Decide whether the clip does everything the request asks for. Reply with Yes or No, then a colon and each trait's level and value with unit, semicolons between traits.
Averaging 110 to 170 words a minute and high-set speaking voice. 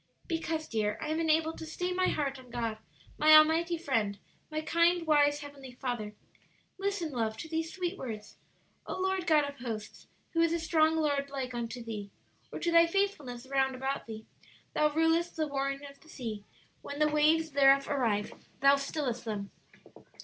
No: average, 180 wpm; very high, 290 Hz